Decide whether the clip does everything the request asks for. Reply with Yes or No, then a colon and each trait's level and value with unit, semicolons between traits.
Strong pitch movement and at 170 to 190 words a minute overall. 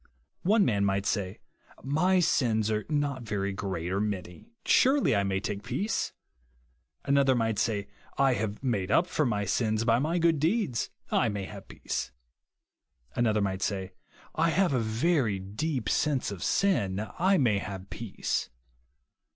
No: wide, 6.6 semitones; average, 160 wpm